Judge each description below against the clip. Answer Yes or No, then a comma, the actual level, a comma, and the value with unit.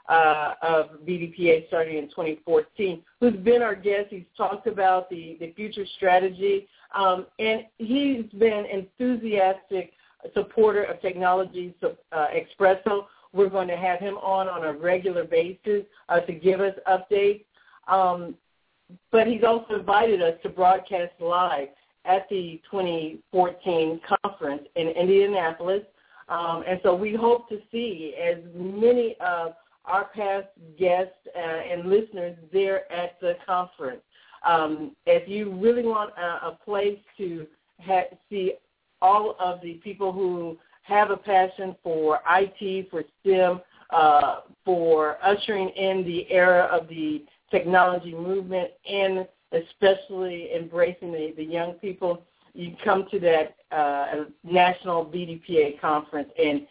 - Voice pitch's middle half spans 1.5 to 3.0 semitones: Yes, average, 2.7 semitones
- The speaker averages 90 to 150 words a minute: Yes, slow, 135 wpm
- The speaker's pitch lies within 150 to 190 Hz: Yes, medium, 185 Hz